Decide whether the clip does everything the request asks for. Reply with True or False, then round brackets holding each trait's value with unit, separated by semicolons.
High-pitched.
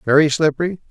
False (155 Hz)